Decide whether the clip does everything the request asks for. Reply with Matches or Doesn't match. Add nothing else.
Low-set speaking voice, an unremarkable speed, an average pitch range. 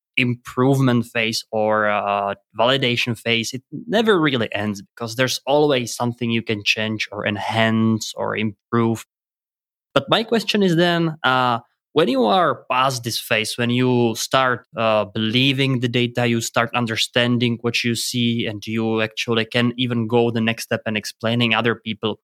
Doesn't match